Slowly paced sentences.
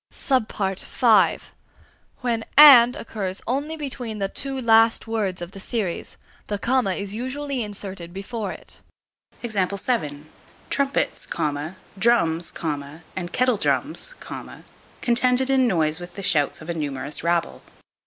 Yes: slow, 115 wpm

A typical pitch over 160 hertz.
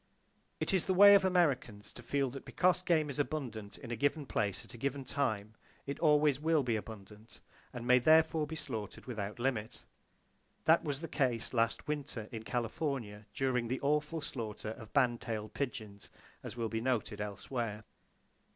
No: low, 125 Hz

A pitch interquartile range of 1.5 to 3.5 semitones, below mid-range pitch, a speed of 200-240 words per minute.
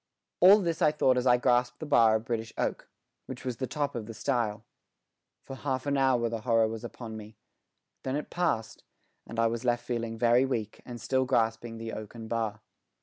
Yes: narrow, 2.6 semitones; low, 120 Hz; fast, 205 wpm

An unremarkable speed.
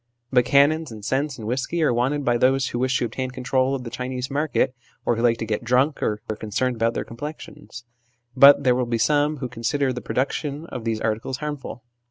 No: fast, 225 wpm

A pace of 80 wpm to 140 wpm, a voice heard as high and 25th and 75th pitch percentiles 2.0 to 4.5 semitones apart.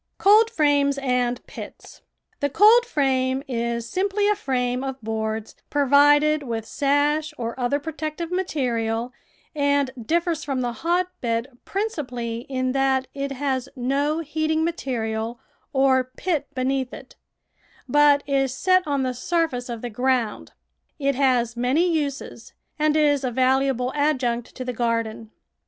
Yes: slow, 135 wpm; very high, 270 Hz; average, 3.4 semitones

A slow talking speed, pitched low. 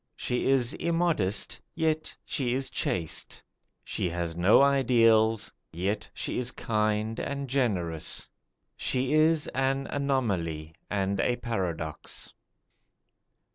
Yes: slow, 105 wpm; low, 115 Hz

